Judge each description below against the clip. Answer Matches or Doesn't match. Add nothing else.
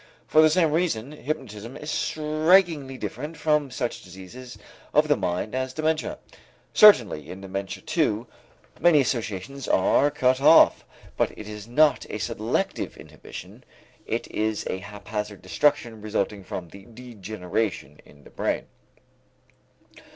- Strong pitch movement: Matches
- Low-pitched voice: Matches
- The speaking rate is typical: Doesn't match